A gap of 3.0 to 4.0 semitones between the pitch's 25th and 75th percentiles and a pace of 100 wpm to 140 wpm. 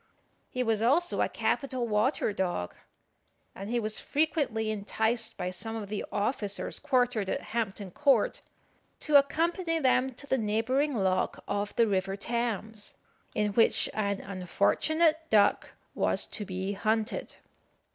No: average, 4.4 semitones; slow, 135 wpm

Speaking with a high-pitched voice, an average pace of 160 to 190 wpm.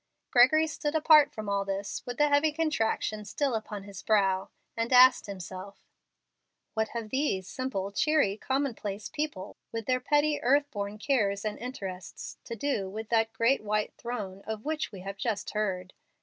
Yes: high, 220 Hz; average, 165 wpm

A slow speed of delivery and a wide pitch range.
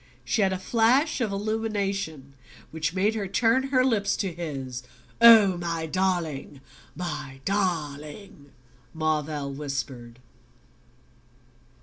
Yes: slow, 105 wpm; wide, 5.9 semitones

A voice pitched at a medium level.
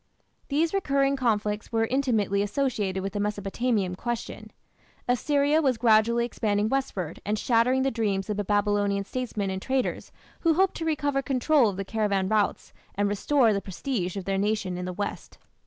No: high, 220 Hz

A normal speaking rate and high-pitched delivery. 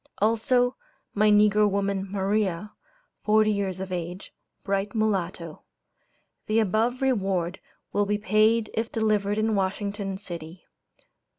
No: slow, 115 wpm; high, 205 Hz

